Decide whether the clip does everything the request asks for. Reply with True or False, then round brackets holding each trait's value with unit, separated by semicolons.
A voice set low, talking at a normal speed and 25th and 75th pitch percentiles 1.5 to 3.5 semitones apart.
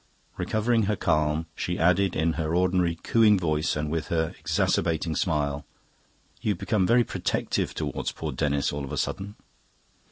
False (85 Hz; 155 wpm; 4.0 semitones)